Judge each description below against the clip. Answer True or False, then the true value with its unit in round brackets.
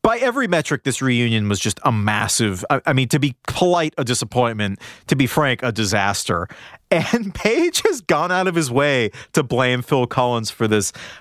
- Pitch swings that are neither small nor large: False (5.7 semitones)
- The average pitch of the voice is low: True (130 Hz)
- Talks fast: False (195 wpm)